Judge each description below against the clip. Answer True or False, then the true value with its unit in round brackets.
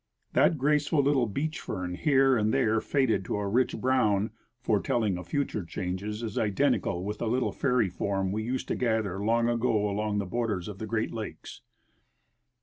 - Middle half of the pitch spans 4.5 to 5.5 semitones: False (3.9 semitones)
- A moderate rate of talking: True (175 wpm)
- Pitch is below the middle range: True (110 Hz)